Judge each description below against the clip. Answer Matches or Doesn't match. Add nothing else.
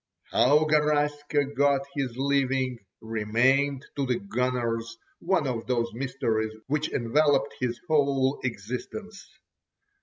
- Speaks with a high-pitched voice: Doesn't match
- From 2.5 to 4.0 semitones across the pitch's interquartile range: Matches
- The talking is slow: Matches